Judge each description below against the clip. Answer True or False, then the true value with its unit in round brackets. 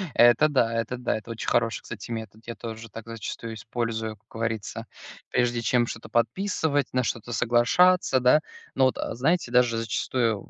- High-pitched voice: False (120 Hz)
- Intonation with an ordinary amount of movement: False (1.9 semitones)